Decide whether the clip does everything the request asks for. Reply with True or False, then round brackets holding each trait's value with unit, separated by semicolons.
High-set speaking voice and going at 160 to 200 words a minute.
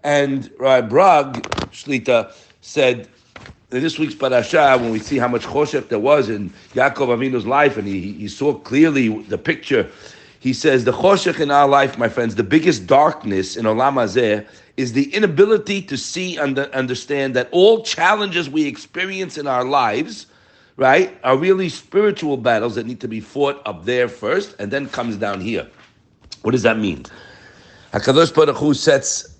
False (135 Hz; 170 wpm)